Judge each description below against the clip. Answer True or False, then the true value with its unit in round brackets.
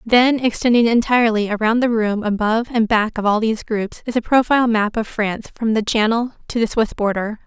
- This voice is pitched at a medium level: False (225 Hz)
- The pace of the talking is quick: True (210 wpm)